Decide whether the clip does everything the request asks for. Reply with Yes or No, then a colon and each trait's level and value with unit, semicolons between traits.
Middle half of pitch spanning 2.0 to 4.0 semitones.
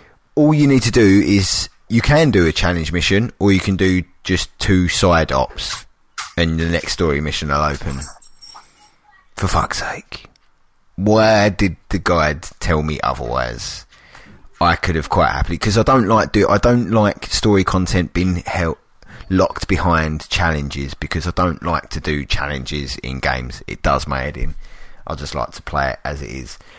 No: average, 5.0 semitones